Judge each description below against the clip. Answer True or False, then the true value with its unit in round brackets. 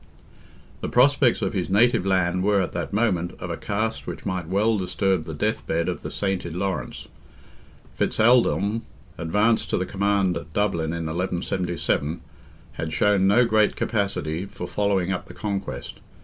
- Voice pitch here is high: False (95 Hz)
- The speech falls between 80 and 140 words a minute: False (165 wpm)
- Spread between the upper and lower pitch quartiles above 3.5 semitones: False (3.1 semitones)